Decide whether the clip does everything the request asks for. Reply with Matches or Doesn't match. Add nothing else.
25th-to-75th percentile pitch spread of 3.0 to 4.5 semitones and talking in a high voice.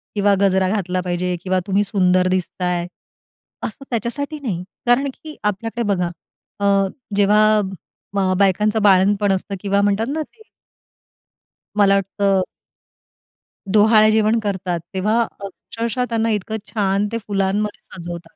Doesn't match